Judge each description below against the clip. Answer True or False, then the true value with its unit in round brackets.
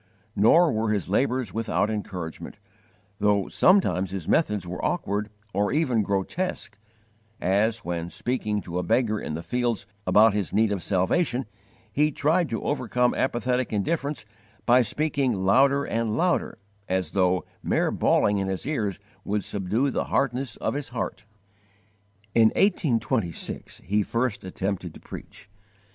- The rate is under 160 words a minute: True (140 wpm)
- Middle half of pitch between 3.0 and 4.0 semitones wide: False (5.0 semitones)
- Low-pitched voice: True (110 Hz)